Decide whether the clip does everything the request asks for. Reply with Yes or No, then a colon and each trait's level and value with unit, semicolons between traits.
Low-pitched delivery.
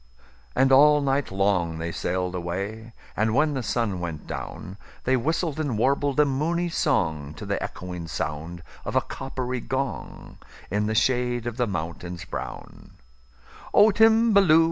Yes: low, 115 Hz